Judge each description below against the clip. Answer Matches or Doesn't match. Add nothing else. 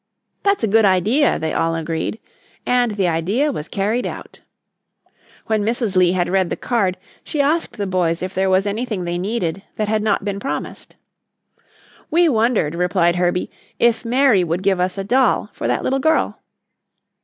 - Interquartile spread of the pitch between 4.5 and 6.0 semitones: Matches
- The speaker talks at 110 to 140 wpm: Doesn't match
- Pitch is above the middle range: Matches